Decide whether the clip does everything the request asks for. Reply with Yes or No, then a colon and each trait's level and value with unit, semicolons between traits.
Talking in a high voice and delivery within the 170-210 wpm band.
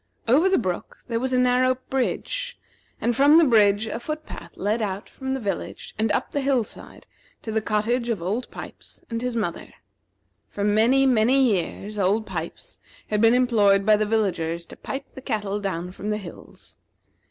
Yes: high, 225 Hz; average, 185 wpm